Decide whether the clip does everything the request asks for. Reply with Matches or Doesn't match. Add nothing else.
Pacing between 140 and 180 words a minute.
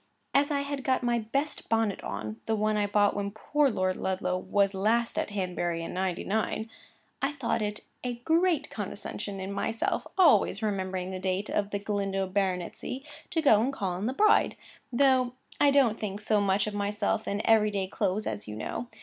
Doesn't match